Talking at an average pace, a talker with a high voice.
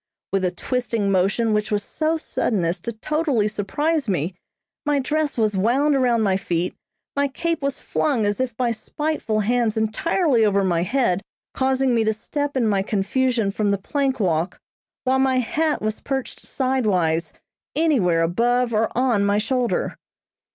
Yes: average, 165 wpm; high, 230 Hz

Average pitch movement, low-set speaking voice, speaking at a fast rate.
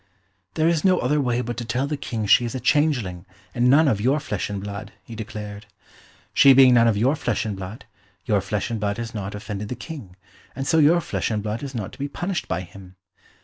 Yes: average, 5.0 semitones; low, 115 Hz; fast, 235 wpm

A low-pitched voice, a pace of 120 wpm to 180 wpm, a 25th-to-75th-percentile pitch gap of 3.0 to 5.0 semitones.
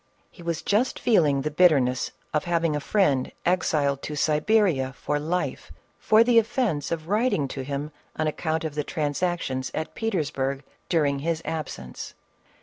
No: medium, 155 Hz; average, 155 wpm; average, 4.0 semitones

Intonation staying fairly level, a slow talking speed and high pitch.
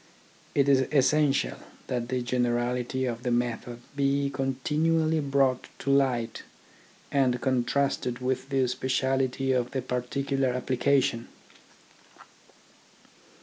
No: narrow, 2.0 semitones; slow, 105 wpm; low, 130 Hz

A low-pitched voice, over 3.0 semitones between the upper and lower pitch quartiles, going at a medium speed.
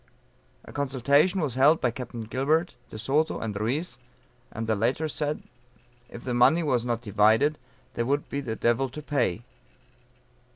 Yes: low, 130 Hz; average, 4.2 semitones; average, 160 wpm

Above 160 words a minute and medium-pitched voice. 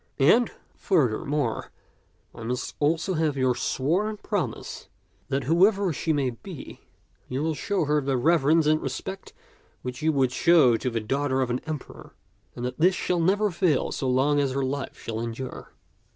Yes: average, 170 wpm; medium, 145 Hz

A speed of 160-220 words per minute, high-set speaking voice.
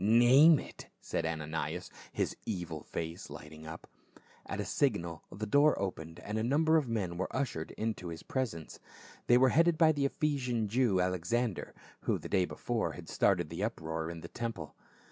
No: average, 175 wpm; low, 100 Hz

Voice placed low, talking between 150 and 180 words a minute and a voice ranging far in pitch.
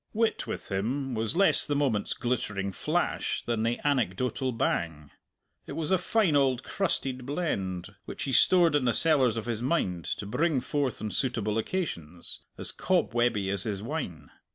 Yes: low, 120 Hz; average, 170 wpm; wide, 6.1 semitones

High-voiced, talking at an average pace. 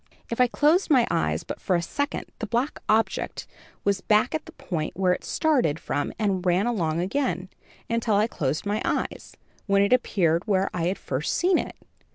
Yes: high, 200 Hz; average, 195 wpm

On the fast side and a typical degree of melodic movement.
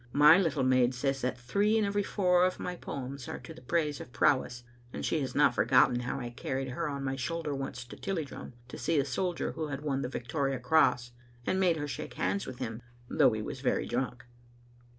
Yes: fast, 225 wpm; average, 4.5 semitones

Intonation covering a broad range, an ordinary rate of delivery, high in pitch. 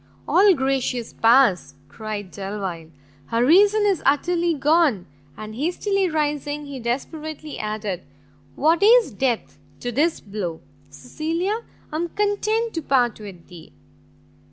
No: wide, 7.9 semitones; slow, 125 wpm; very high, 275 Hz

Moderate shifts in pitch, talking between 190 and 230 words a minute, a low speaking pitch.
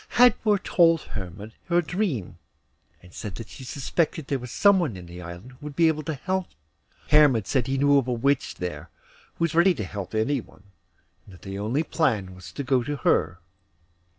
No: wide, 8.0 semitones; fast, 205 wpm; low, 130 Hz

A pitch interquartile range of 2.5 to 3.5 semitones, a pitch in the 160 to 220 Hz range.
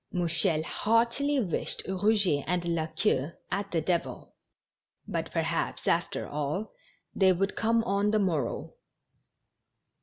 No: average, 4.6 semitones; medium, 185 Hz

